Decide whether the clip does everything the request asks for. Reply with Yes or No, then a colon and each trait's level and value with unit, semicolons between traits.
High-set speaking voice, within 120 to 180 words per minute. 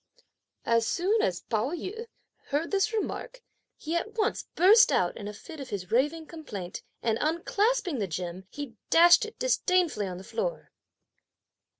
Yes: very high, 320 Hz; average, 160 wpm